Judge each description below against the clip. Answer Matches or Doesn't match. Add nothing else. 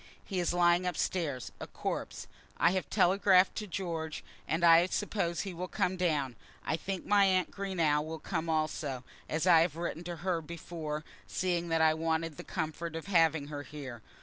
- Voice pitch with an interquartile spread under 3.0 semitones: Matches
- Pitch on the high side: Doesn't match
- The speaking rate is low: Doesn't match